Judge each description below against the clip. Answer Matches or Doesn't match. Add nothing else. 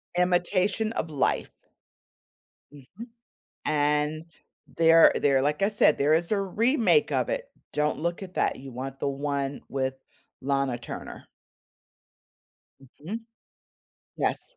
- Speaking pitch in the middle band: Matches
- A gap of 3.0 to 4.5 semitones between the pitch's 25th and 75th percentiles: Doesn't match